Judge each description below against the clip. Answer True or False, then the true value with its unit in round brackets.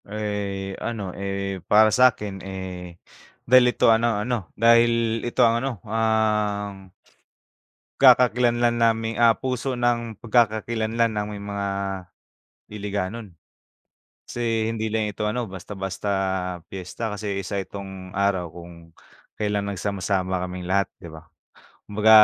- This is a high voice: False (105 Hz)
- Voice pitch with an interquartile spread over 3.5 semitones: False (2.9 semitones)